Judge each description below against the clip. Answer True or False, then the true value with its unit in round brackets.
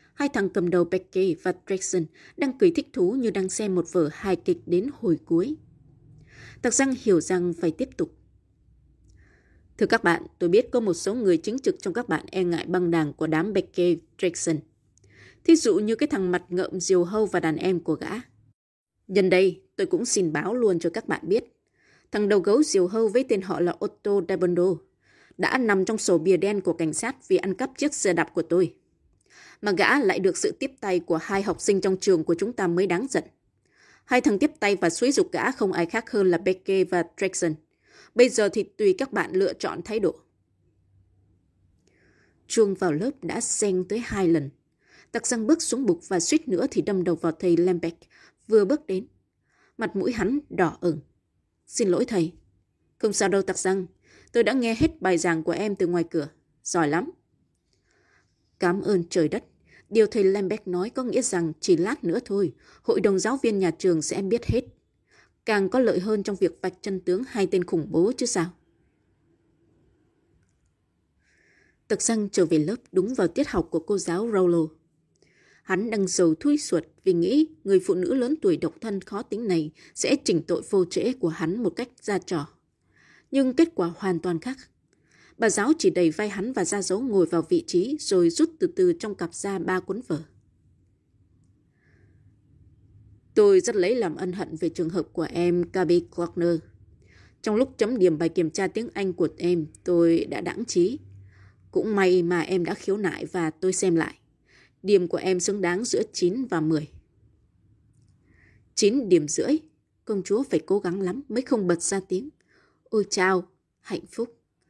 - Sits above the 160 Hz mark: True (185 Hz)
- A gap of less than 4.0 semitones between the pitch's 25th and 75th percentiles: False (5.1 semitones)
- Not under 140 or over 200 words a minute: True (195 wpm)